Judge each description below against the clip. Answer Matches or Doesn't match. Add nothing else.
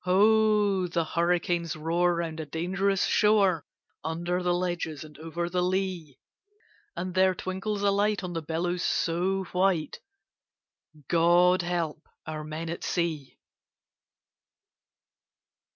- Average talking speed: Doesn't match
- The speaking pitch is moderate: Matches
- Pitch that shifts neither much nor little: Doesn't match